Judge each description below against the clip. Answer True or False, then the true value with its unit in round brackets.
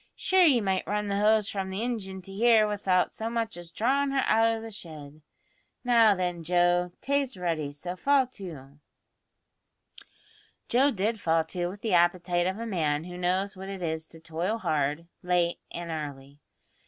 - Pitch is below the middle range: False (185 Hz)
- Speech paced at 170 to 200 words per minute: True (180 wpm)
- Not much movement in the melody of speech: False (4.6 semitones)